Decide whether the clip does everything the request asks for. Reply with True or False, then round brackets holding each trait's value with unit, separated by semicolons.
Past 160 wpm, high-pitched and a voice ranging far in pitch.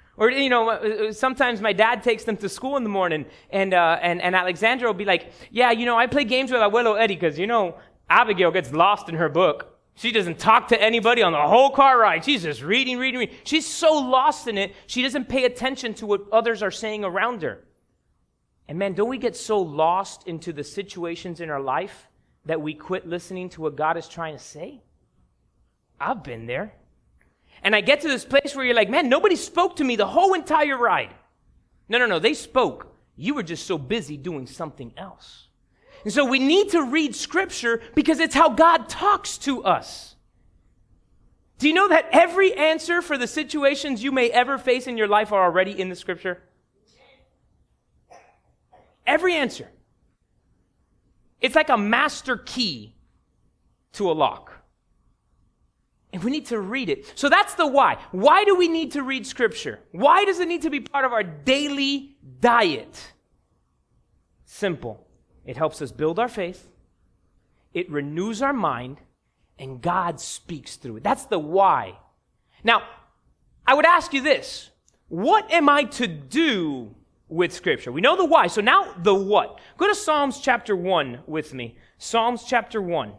True (180 wpm; 230 Hz; 7.7 semitones)